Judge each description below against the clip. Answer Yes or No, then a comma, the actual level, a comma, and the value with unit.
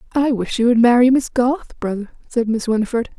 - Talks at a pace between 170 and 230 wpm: Yes, fast, 205 wpm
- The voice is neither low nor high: No, high, 240 Hz